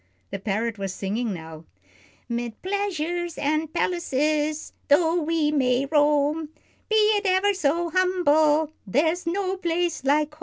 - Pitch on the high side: Yes, very high, 310 Hz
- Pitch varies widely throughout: No, average, 4.1 semitones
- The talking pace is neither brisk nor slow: No, slow, 130 wpm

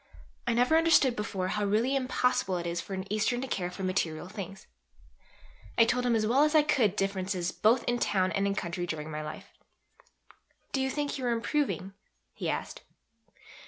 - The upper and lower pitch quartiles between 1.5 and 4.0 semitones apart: No, average, 5.2 semitones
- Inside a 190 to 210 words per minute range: Yes, average, 195 wpm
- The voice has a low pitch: No, high, 210 Hz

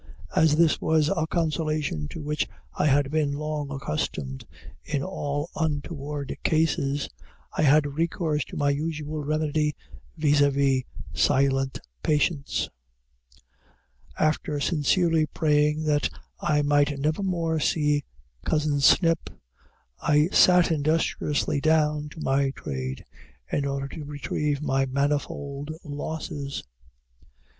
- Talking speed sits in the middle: No, slow, 110 wpm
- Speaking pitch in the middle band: Yes, medium, 150 Hz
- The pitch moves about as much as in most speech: No, narrow, 1.7 semitones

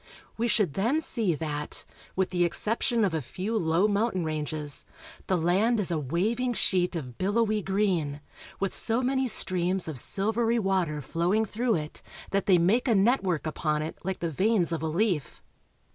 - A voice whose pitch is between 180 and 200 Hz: Yes, high, 190 Hz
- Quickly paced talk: No, average, 175 wpm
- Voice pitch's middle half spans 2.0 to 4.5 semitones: No, average, 5.3 semitones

